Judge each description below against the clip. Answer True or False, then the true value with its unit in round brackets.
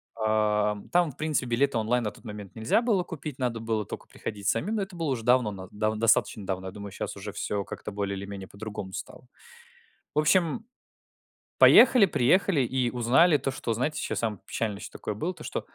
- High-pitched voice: False (115 Hz)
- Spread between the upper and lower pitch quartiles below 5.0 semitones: False (6.4 semitones)